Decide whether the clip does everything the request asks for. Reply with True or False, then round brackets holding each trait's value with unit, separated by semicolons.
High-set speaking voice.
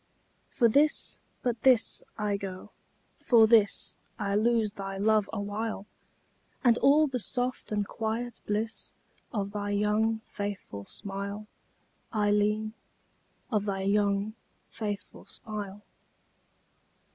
True (210 Hz)